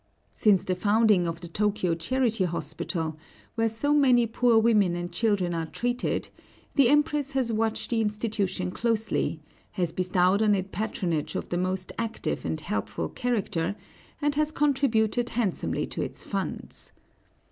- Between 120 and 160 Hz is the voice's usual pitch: No, high, 215 Hz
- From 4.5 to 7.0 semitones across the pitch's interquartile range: Yes, average, 4.8 semitones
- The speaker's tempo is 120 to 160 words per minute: Yes, average, 145 wpm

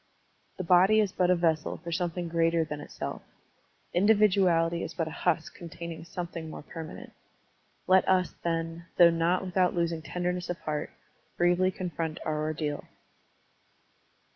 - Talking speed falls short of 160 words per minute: Yes, average, 145 wpm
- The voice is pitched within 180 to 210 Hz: No, medium, 170 Hz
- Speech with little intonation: Yes, narrow, 1.7 semitones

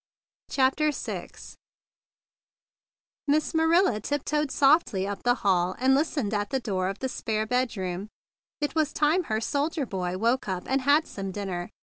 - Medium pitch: No, very high, 250 Hz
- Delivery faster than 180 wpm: No, average, 150 wpm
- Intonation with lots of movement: Yes, wide, 6.8 semitones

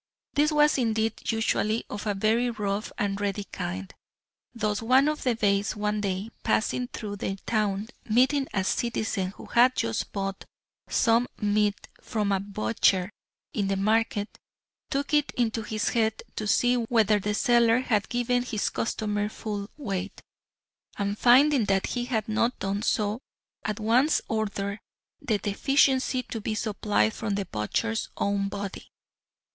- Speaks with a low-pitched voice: No, high, 215 Hz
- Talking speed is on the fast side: No, average, 150 wpm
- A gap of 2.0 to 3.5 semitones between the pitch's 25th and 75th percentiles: Yes, average, 2.9 semitones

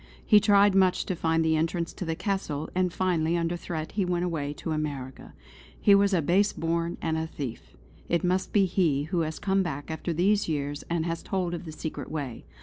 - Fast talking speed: Yes, fast, 215 wpm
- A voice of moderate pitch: Yes, medium, 170 Hz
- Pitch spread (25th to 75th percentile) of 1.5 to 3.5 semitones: Yes, average, 2.8 semitones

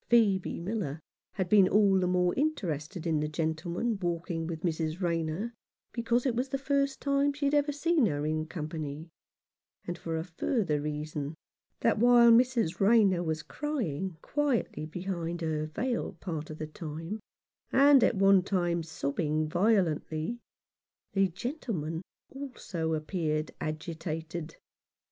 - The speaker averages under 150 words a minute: Yes, average, 140 wpm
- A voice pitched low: No, medium, 175 Hz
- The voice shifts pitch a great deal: Yes, wide, 6.6 semitones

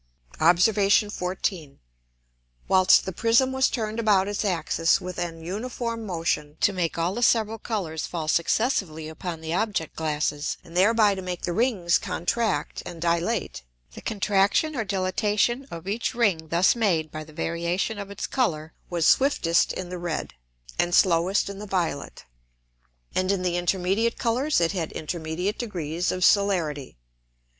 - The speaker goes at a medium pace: Yes, average, 155 wpm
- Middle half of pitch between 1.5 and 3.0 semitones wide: No, average, 4.1 semitones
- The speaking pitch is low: No, medium, 185 Hz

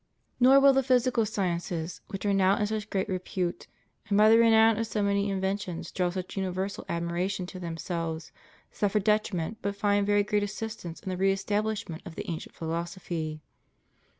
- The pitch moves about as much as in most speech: Yes, average, 3.1 semitones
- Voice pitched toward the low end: No, high, 195 Hz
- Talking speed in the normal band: Yes, average, 175 wpm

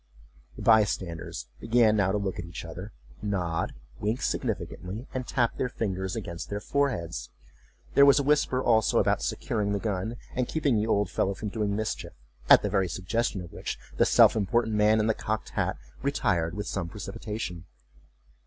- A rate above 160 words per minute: Yes, average, 180 wpm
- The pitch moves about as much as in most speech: Yes, average, 3.7 semitones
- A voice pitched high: No, low, 105 Hz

